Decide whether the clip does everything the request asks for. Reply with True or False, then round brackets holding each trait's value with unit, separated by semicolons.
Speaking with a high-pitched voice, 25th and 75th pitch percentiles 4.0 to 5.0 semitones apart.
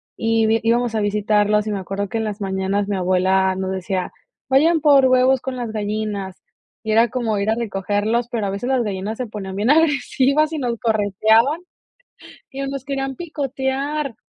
True (220 Hz; 4.7 semitones)